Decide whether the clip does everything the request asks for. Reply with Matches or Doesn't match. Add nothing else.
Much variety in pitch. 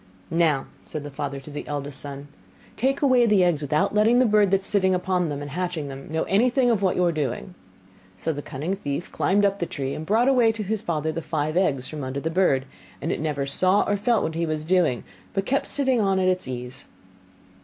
Matches